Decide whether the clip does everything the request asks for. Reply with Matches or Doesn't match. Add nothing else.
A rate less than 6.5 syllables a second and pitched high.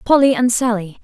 Matches